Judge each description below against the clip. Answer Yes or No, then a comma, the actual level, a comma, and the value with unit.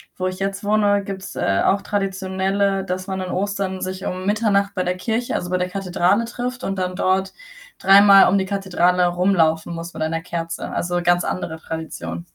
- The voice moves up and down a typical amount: No, narrow, 1.9 semitones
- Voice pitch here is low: No, high, 190 Hz